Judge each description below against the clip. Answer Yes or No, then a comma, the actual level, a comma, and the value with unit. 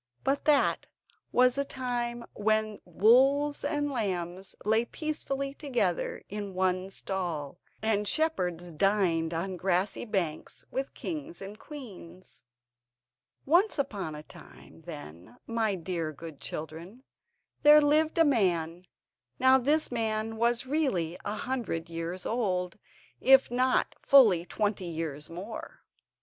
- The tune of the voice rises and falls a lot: Yes, wide, 6.9 semitones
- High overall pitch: Yes, high, 210 Hz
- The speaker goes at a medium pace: No, slow, 120 wpm